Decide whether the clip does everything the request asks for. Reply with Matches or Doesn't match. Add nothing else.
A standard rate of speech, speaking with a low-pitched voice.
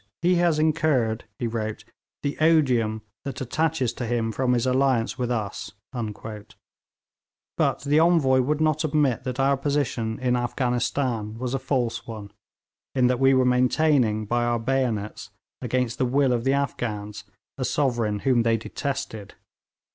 Matches